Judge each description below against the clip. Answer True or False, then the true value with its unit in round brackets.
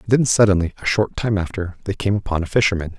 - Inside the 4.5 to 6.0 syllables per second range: False (6.5 syllables/s)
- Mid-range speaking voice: False (100 Hz)